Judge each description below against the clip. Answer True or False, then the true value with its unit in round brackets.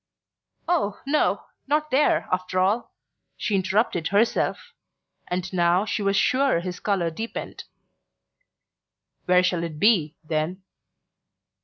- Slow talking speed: True (115 wpm)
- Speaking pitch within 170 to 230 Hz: True (190 Hz)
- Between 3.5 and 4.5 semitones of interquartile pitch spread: True (3.9 semitones)